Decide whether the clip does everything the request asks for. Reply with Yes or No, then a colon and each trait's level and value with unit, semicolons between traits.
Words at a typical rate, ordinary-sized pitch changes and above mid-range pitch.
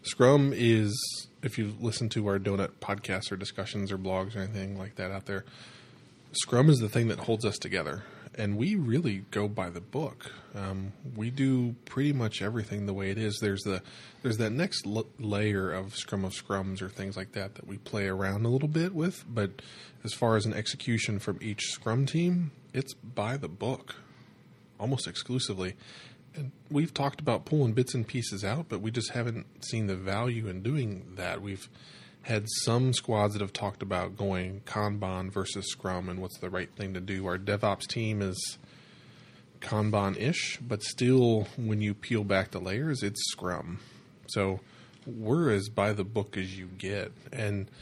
No: average, 185 wpm; average, 4.1 semitones; low, 105 Hz